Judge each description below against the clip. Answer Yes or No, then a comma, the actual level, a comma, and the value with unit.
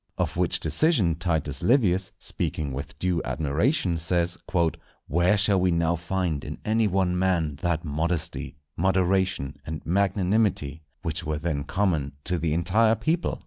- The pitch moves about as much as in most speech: Yes, average, 3.3 semitones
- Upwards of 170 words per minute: No, average, 145 wpm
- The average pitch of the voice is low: Yes, very low, 85 Hz